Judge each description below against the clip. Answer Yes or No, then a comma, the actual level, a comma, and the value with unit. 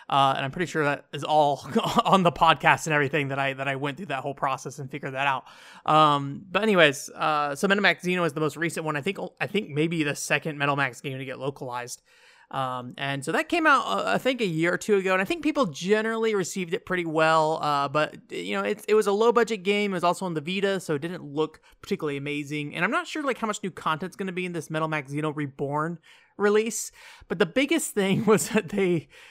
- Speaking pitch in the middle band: Yes, medium, 160 Hz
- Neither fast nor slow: No, fast, 250 wpm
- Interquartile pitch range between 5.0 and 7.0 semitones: Yes, wide, 5.4 semitones